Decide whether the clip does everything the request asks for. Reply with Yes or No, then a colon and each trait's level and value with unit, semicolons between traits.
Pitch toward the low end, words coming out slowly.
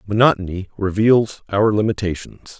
Yes: low, 105 Hz; slow, 95 wpm